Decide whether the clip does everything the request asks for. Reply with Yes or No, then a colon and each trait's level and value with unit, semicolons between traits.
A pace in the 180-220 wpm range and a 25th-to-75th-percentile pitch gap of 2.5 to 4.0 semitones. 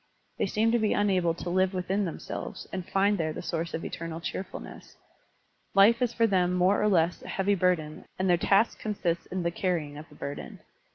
Yes: fast, 205 wpm; average, 3.1 semitones